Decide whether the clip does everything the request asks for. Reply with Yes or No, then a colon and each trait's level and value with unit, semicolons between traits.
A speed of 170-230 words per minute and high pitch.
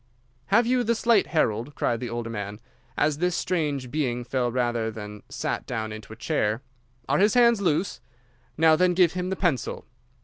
No: average, 180 wpm; medium, 145 Hz